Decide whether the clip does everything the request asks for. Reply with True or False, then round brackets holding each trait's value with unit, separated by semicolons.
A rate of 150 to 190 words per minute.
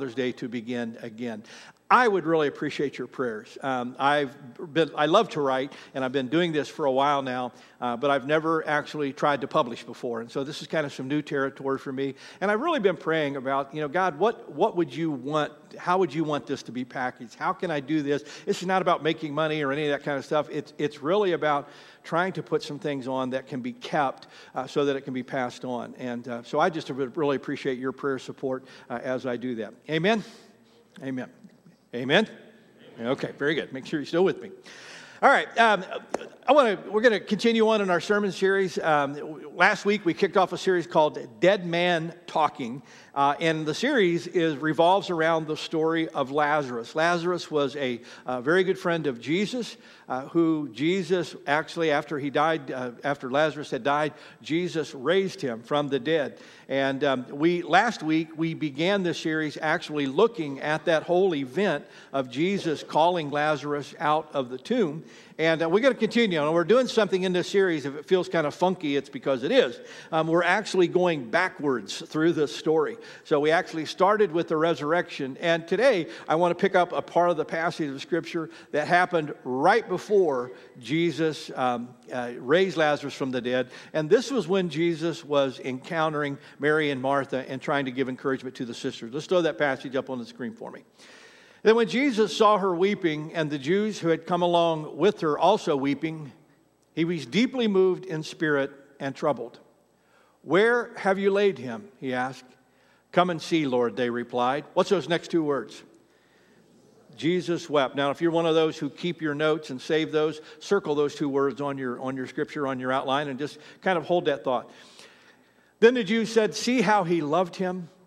False (205 wpm)